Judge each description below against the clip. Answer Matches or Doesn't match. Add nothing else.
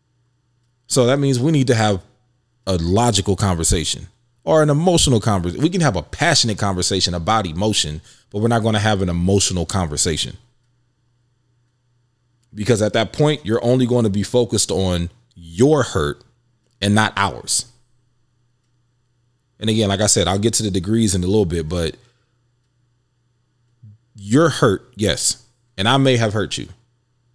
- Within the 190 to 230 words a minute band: Doesn't match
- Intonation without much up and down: Doesn't match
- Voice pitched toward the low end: Matches